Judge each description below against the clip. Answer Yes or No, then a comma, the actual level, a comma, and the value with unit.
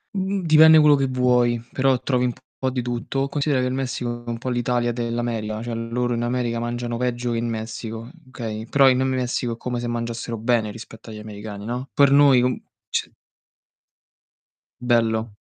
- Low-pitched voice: Yes, low, 120 Hz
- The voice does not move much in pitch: Yes, narrow, 1.8 semitones